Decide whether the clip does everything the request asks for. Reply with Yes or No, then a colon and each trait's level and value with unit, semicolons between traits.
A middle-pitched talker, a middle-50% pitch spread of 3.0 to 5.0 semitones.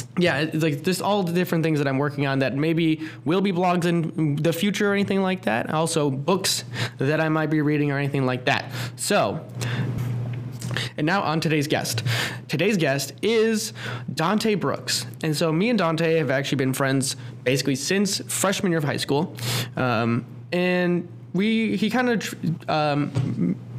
No: medium, 150 Hz; wide, 5.5 semitones